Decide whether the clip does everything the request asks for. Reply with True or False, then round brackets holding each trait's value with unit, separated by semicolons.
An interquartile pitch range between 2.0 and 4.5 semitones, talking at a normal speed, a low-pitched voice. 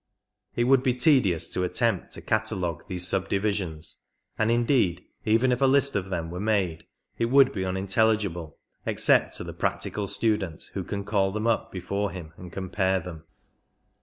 True (3.9 semitones; 165 wpm; 100 Hz)